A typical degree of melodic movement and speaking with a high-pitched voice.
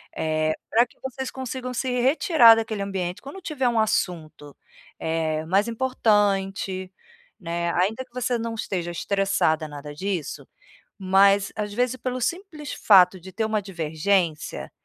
No: wide, 5.9 semitones; high, 200 Hz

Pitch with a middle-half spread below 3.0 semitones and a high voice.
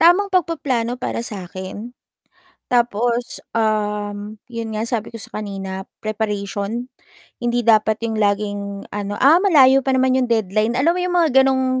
No: average, 3.8 semitones; high, 230 Hz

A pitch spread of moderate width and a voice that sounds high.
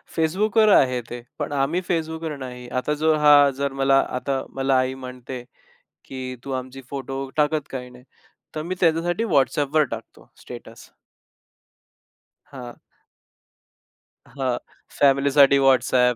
No: average, 3.4 semitones; low, 135 Hz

